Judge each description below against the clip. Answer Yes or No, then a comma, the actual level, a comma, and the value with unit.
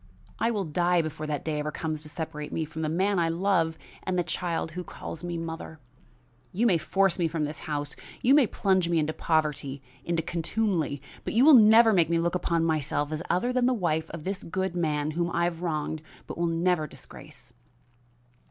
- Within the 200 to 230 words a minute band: Yes, fast, 205 wpm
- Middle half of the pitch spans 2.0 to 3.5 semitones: Yes, average, 2.9 semitones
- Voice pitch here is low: No, medium, 165 Hz